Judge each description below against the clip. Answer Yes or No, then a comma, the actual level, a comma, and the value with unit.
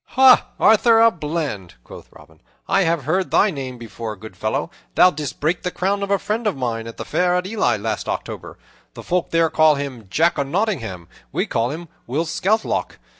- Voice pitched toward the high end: No, medium, 155 Hz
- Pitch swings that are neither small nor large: No, wide, 8.2 semitones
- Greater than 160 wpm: Yes, average, 200 wpm